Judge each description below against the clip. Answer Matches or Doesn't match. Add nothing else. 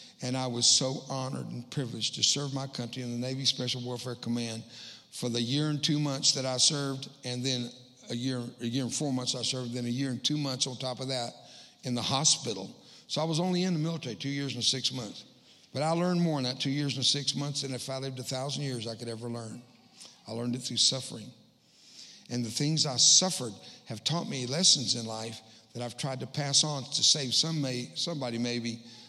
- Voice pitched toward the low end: Matches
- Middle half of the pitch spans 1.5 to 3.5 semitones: Matches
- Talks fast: Matches